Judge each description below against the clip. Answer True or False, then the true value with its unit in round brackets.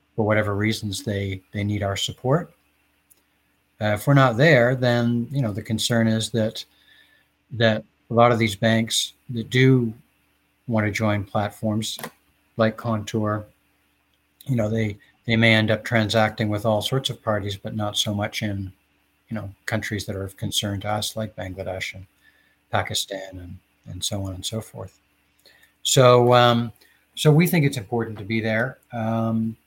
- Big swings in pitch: False (2.8 semitones)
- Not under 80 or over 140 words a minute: False (170 wpm)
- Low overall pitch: True (110 Hz)